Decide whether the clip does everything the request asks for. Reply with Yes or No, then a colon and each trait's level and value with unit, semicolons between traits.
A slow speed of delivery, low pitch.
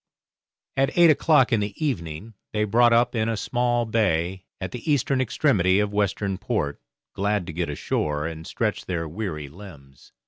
No: average, 170 wpm; low, 105 Hz